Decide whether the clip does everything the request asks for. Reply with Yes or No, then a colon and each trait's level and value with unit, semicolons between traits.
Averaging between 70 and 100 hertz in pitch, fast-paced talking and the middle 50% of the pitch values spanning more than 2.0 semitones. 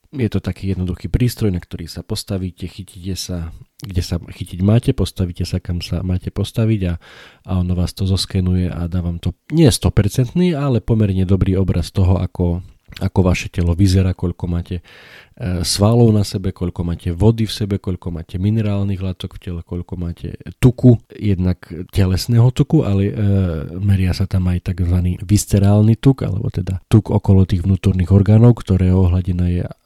Yes: very low, 95 Hz; fast, 170 wpm; average, 2.7 semitones